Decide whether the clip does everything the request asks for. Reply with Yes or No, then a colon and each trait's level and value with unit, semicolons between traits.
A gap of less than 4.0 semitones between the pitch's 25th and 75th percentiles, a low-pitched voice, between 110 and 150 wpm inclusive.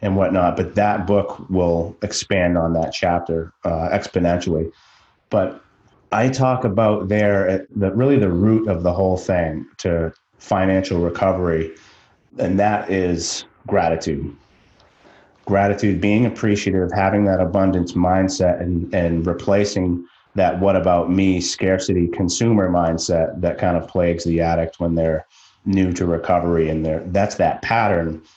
Yes: average, 2.9 semitones; very low, 95 Hz; average, 140 wpm